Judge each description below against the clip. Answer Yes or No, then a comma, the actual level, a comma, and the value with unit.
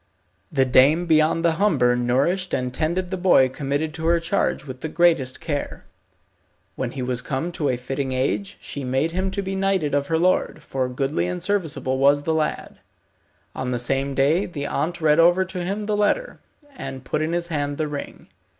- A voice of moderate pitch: Yes, medium, 155 Hz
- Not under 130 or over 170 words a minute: No, average, 195 wpm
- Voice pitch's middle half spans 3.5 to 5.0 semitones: Yes, average, 4.7 semitones